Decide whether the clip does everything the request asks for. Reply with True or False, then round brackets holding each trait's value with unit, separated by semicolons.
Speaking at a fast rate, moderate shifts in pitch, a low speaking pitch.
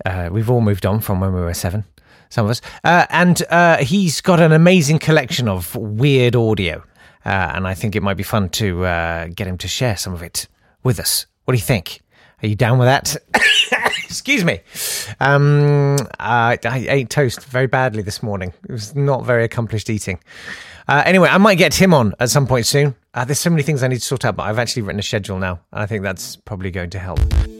False (230 wpm; 6.3 semitones; 115 Hz)